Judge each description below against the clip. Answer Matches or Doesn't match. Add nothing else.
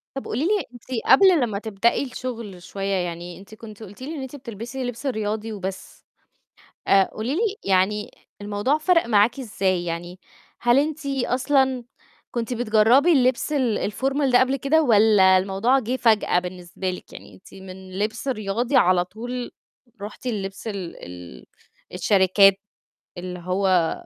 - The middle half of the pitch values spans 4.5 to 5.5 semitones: Matches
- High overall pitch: Matches